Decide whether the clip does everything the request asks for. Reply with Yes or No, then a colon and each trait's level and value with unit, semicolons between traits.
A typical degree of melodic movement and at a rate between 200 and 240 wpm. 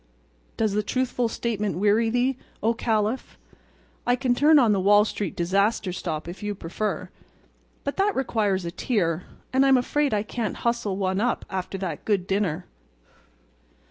No: average, 4.2 semitones; average, 160 wpm